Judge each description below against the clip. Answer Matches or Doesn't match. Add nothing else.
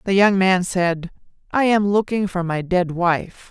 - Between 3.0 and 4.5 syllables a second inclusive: Matches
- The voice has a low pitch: Doesn't match